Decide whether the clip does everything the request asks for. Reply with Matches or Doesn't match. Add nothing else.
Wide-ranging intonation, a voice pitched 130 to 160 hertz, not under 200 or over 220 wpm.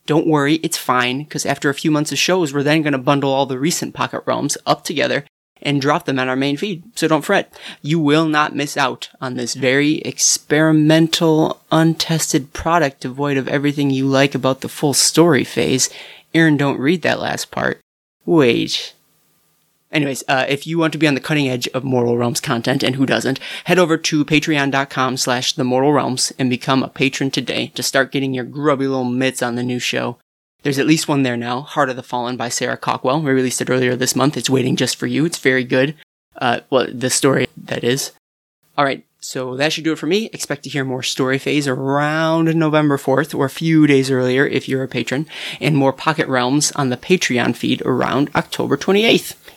Doesn't match